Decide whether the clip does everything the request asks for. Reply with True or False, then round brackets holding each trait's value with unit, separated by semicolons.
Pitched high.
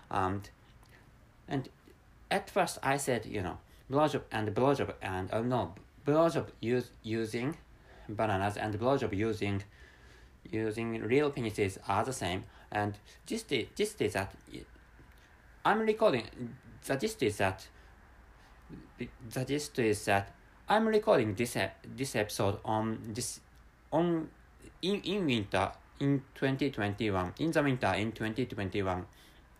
False (110 Hz)